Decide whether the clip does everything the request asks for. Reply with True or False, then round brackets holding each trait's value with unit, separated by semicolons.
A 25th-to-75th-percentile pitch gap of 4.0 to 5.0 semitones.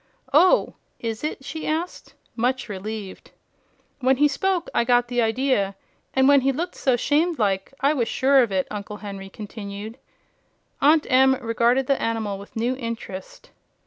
True (4.5 semitones)